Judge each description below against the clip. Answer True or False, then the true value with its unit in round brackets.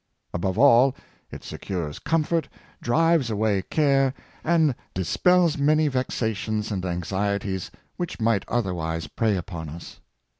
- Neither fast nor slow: False (115 wpm)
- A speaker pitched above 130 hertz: False (110 Hz)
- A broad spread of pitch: True (7.3 semitones)